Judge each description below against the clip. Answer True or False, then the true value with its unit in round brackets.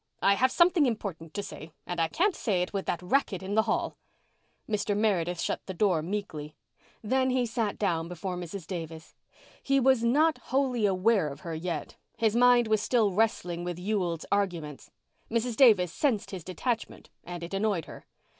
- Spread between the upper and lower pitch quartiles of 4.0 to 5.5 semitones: True (4.9 semitones)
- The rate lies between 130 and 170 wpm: False (180 wpm)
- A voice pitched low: False (200 Hz)